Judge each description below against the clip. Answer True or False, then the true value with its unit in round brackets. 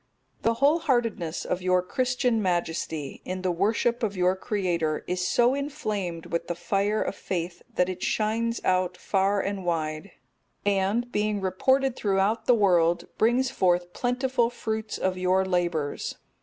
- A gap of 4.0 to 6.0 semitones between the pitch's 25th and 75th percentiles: True (4.4 semitones)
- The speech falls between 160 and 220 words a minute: False (150 wpm)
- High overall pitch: True (195 Hz)